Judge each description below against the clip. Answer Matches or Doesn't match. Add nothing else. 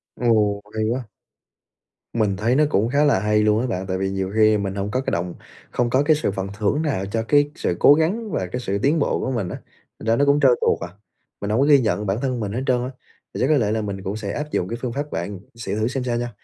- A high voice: Doesn't match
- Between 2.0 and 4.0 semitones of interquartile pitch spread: Doesn't match